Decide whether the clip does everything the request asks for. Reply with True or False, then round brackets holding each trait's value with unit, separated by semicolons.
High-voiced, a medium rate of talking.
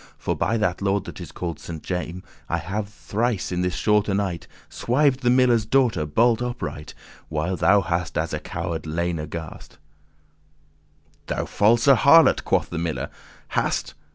False (95 Hz; 165 wpm)